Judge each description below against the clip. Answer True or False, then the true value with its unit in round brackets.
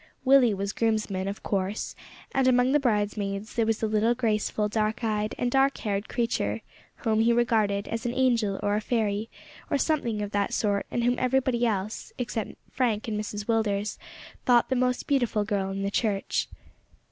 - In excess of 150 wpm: True (180 wpm)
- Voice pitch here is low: False (220 Hz)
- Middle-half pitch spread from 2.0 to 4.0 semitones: True (2.8 semitones)